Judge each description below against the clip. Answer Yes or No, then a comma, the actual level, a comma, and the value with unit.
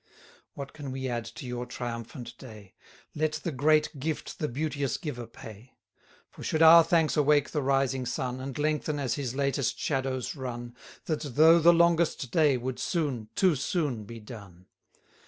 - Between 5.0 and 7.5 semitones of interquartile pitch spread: No, average, 4.1 semitones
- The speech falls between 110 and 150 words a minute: No, average, 165 wpm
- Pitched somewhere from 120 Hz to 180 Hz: Yes, low, 135 Hz